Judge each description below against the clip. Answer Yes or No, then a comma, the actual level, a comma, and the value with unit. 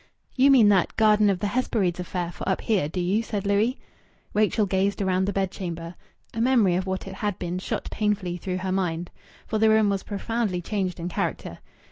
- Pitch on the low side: No, high, 195 Hz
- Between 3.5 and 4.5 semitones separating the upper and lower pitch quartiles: No, average, 2.7 semitones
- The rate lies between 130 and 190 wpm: No, average, 200 wpm